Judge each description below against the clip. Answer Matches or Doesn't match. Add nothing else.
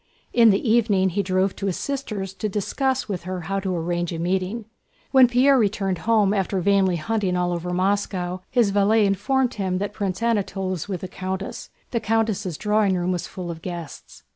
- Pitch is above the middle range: Matches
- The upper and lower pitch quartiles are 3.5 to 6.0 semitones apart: Doesn't match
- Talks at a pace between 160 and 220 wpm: Matches